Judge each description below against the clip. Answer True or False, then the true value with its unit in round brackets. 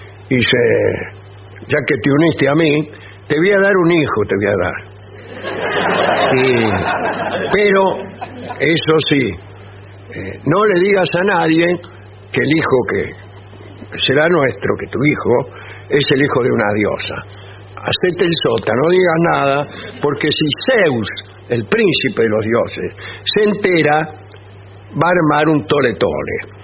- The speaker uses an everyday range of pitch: False (8.1 semitones)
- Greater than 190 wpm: False (145 wpm)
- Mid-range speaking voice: False (130 Hz)